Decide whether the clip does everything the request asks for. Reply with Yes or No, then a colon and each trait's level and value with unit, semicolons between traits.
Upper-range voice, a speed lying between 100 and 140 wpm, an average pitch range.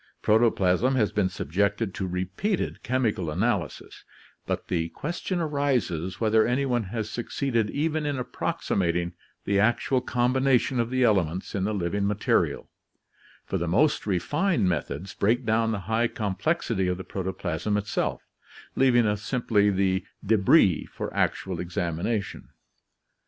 No: low, 105 Hz; slow, 135 wpm; average, 4.9 semitones